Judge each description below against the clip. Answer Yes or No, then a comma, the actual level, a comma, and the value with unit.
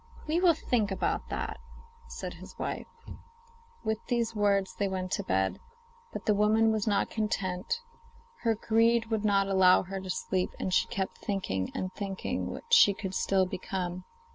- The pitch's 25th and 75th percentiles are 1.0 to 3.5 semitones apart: Yes, average, 2.8 semitones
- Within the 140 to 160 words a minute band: No, average, 170 wpm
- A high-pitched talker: Yes, high, 200 Hz